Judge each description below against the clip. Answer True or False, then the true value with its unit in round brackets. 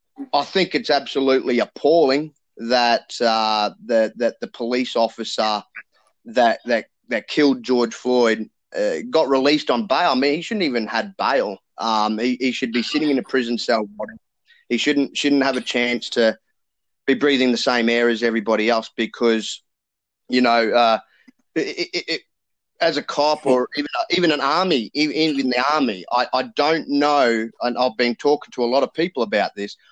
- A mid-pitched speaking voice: False (125 Hz)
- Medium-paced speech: True (180 wpm)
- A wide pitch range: False (3.9 semitones)